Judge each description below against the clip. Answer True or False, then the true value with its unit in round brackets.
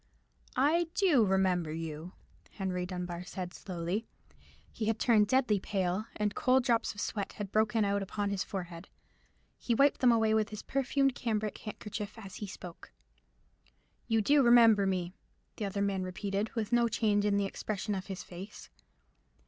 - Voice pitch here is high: True (205 Hz)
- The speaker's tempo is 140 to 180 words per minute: True (165 wpm)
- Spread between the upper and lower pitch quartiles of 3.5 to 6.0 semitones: False (3.1 semitones)